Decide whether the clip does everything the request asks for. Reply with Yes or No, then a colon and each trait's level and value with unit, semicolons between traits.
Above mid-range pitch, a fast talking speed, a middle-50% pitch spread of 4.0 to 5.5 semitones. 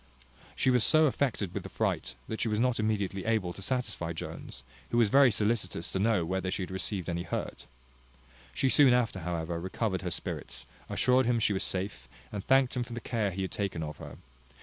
No: low, 105 Hz; fast, 210 wpm; average, 4.6 semitones